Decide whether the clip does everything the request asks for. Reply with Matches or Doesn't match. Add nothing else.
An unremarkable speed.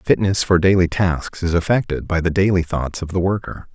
Doesn't match